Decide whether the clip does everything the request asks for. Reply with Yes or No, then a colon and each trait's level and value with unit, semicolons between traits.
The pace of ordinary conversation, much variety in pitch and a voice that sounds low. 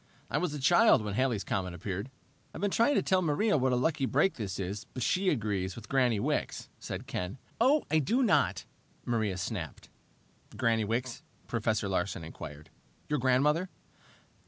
Yes: average, 170 wpm; wide, 7.1 semitones; low, 120 Hz